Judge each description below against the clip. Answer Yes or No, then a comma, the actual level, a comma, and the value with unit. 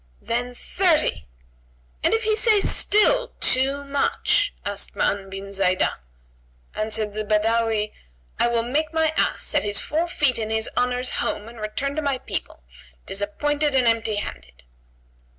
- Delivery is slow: No, average, 150 wpm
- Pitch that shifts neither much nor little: No, wide, 5.9 semitones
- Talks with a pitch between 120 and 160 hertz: No, high, 235 Hz